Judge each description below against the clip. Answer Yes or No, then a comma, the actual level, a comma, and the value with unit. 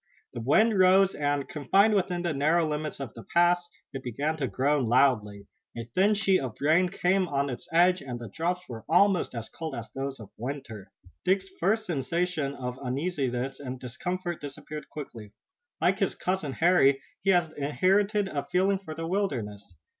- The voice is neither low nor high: Yes, medium, 155 Hz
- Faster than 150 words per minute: Yes, average, 175 wpm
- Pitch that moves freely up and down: Yes, wide, 5.7 semitones